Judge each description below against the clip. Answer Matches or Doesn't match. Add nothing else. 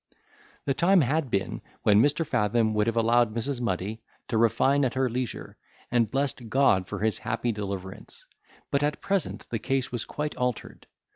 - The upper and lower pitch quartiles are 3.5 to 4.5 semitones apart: Matches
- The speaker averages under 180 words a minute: Matches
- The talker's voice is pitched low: Matches